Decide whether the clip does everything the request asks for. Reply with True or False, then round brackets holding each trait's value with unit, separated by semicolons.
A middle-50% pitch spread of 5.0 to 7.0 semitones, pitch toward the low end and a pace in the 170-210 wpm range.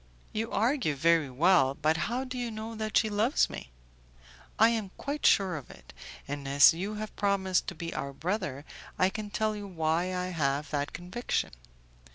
False (5.5 semitones; 185 Hz; 185 wpm)